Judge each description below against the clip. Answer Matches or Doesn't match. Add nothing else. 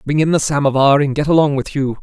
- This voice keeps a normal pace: Doesn't match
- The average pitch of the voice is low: Doesn't match